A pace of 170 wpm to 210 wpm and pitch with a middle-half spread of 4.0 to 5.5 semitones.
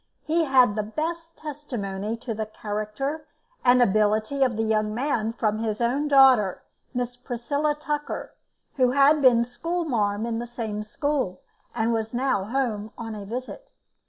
No: average, 160 wpm; average, 4.4 semitones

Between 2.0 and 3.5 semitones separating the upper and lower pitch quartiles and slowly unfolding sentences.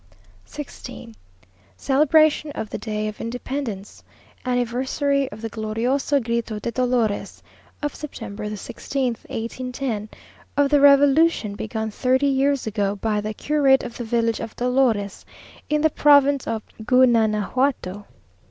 No: average, 4.2 semitones; slow, 125 wpm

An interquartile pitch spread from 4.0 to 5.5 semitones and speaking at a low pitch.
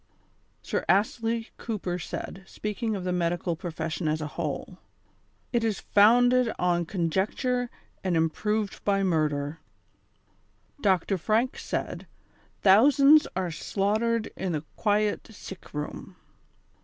No: average, 4.7 semitones; high, 195 Hz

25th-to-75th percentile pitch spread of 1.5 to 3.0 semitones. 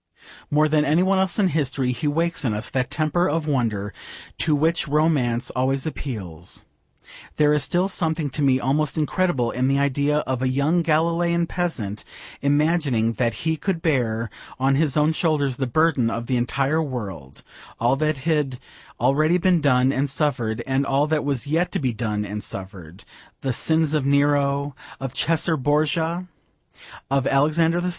No: average, 3.9 semitones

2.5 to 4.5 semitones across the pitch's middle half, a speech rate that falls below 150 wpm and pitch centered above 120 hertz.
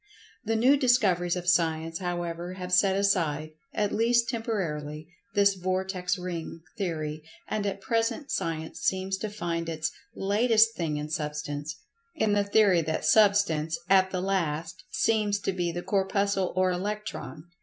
Yes: average, 3.7 semitones; average, 140 wpm; medium, 185 Hz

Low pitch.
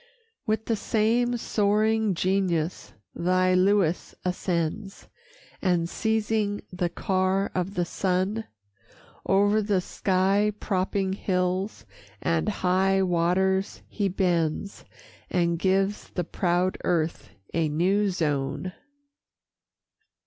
No: high, 190 Hz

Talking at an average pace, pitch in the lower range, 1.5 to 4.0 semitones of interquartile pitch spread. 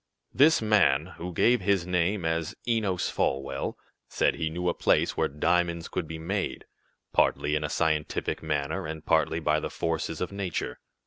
Yes: average, 170 wpm; very low, 85 Hz; average, 2.8 semitones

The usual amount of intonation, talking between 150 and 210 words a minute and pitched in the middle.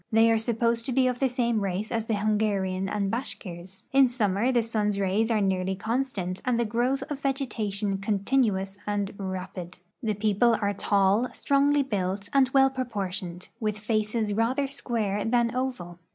No: average, 3.8 semitones; average, 165 wpm; high, 215 Hz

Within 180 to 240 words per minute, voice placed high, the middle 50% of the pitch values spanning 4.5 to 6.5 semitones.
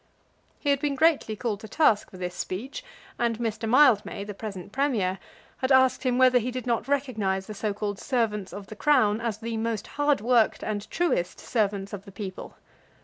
No: average, 195 wpm; high, 220 Hz; average, 4.1 semitones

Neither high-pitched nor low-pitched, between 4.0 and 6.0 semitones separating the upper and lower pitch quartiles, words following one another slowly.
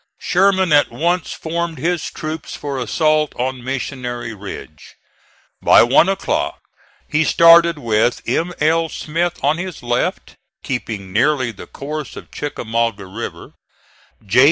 Yes: medium, 145 Hz; wide, 5.6 semitones; slow, 130 wpm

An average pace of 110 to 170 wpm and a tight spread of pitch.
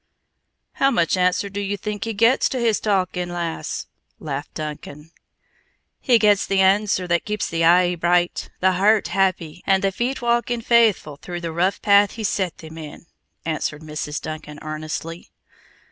No: average, 160 wpm; average, 4.1 semitones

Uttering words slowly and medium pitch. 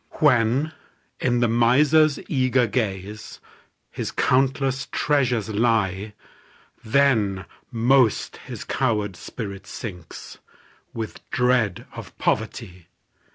No: slow, 85 wpm; low, 120 Hz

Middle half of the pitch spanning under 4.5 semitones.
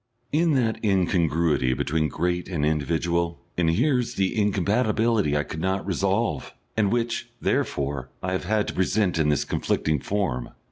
No: average, 5.3 semitones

